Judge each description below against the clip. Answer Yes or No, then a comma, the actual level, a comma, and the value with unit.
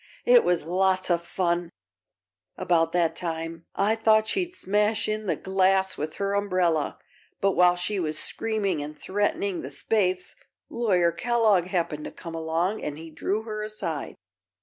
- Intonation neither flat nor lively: Yes, average, 3.9 semitones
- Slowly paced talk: No, average, 155 wpm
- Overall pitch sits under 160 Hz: No, medium, 185 Hz